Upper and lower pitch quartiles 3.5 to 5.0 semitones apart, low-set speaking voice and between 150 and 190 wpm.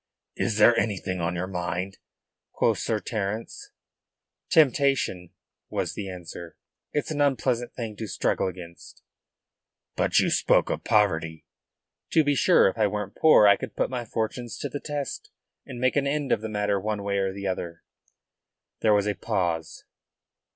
Yes: average, 4.7 semitones; low, 105 Hz; average, 165 wpm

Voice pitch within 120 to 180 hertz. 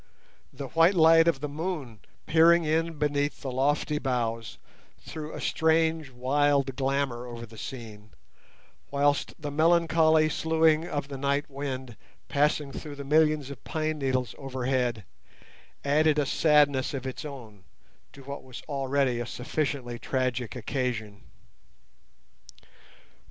Yes: medium, 140 Hz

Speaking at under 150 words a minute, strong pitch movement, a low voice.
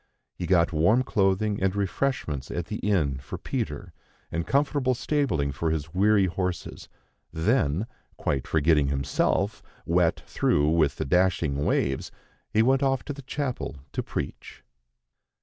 Yes: average, 140 wpm; wide, 6.5 semitones; very low, 90 Hz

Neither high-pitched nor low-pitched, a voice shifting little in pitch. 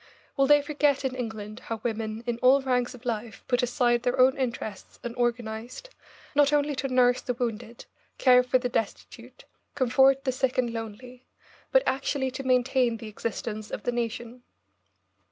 No: high, 245 Hz; narrow, 2.2 semitones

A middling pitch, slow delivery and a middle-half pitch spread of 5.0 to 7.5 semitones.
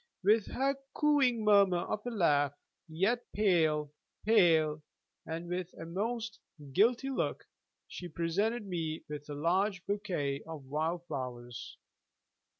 Yes: medium, 180 Hz; slow, 120 wpm; wide, 5.4 semitones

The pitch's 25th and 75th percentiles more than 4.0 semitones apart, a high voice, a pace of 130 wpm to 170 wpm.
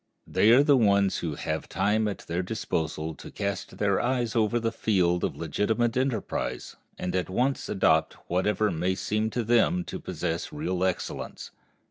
No: average, 4.4 semitones; low, 105 Hz; average, 165 wpm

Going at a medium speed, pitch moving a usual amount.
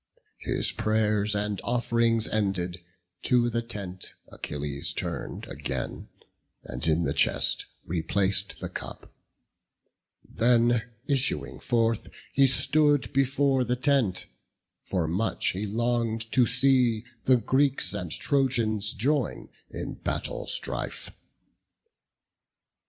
No: slow, 105 wpm; average, 4.3 semitones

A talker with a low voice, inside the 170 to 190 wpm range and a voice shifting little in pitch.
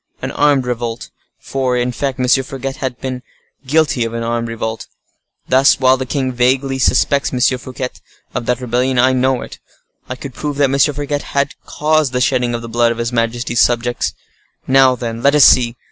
Yes: low, 130 Hz; average, 180 wpm; narrow, 2.1 semitones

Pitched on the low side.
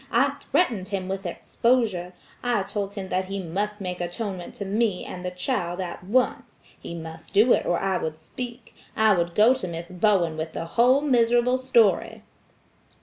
No: high, 195 Hz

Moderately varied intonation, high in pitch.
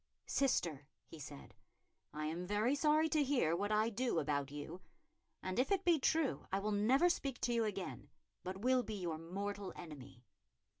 No: wide, 7.8 semitones; high, 205 Hz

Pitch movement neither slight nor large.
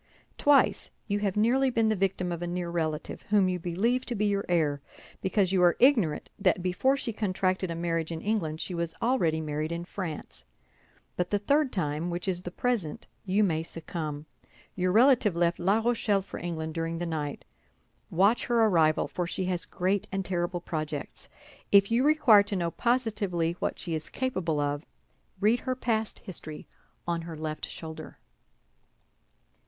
Yes: average, 4.2 semitones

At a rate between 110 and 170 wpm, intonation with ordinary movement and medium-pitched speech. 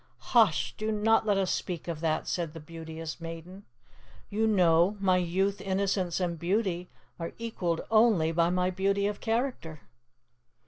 Yes: average, 150 wpm; average, 3.4 semitones; medium, 180 Hz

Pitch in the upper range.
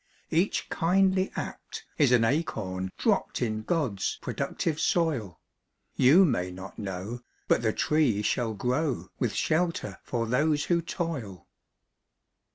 No: low, 125 Hz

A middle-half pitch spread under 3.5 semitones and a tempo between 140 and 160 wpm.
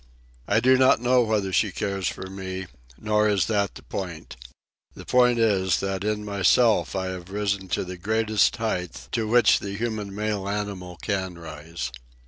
No: average, 2.7 semitones; average, 170 wpm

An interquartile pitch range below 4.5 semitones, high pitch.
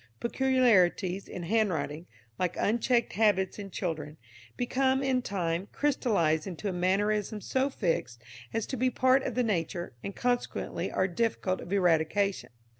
No: wide, 5.5 semitones; high, 200 Hz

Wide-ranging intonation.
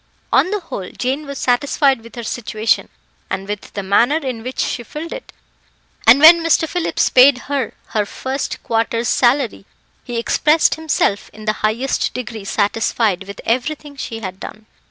No: average, 4.7 semitones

